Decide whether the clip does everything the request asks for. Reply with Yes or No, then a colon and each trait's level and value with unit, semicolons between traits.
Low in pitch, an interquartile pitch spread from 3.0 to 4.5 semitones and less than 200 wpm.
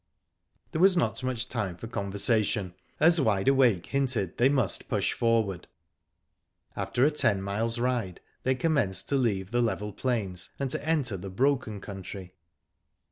No: low, 115 Hz; average, 5.1 semitones; average, 150 wpm